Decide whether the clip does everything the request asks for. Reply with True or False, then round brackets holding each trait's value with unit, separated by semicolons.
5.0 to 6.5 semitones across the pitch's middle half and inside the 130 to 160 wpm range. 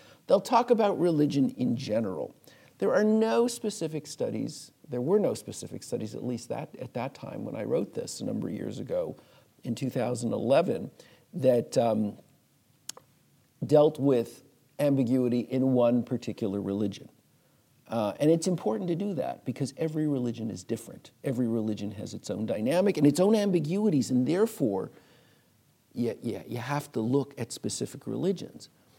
True (5.5 semitones; 155 wpm)